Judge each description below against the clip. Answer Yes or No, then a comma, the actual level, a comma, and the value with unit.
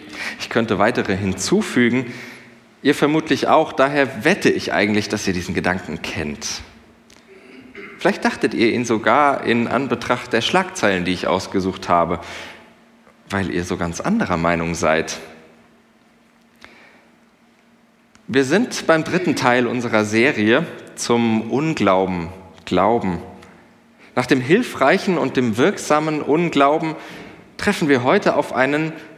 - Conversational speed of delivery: No, slow, 120 wpm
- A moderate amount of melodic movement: No, wide, 7.0 semitones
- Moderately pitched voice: No, low, 115 Hz